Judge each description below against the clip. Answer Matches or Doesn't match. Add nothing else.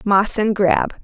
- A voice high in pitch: Matches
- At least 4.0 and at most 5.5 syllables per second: Doesn't match